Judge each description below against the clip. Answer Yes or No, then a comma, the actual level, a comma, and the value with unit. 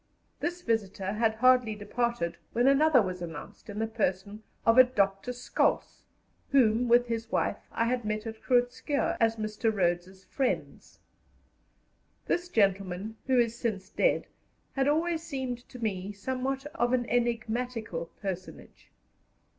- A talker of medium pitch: No, high, 230 Hz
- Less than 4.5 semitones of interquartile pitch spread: Yes, average, 3.8 semitones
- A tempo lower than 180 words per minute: Yes, average, 140 wpm